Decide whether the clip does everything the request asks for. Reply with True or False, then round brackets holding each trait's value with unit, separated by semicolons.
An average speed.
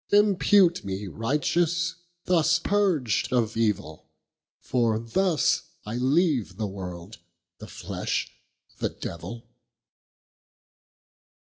False (90 wpm)